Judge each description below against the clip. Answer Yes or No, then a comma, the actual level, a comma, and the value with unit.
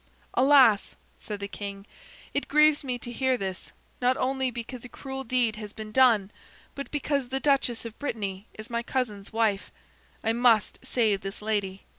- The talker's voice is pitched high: Yes, high, 235 Hz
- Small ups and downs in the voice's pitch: No, average, 3.9 semitones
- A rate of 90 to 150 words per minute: No, average, 170 wpm